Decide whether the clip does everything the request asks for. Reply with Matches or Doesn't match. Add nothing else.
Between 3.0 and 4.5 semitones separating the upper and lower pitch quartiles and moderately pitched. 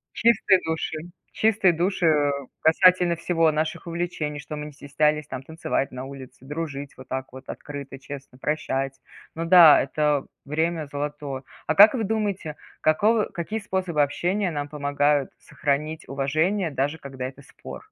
Matches